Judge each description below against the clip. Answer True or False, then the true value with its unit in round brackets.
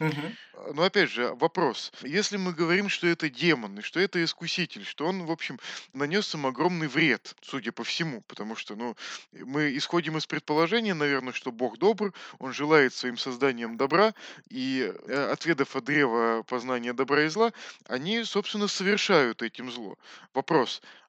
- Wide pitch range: True (6.6 semitones)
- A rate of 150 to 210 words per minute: True (155 wpm)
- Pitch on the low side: False (160 Hz)